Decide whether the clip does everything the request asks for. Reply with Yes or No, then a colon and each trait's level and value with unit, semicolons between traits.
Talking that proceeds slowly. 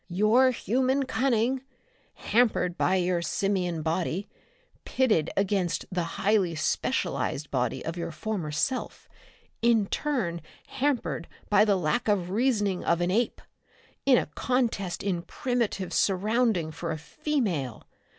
Yes: slow, 125 wpm